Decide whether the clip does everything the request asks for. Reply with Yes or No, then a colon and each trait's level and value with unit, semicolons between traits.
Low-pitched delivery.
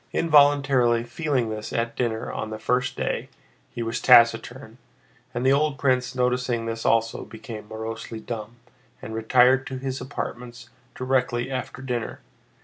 Yes: low, 120 Hz